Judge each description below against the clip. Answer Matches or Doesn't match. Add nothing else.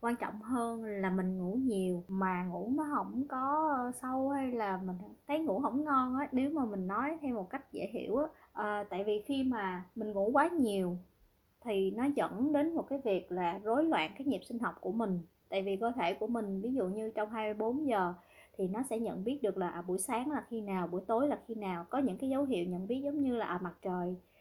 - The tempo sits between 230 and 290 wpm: Matches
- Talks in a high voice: Matches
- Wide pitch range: Matches